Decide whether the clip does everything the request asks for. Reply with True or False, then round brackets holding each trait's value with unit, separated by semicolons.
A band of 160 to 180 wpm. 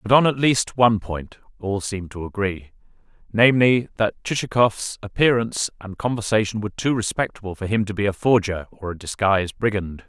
True (165 wpm)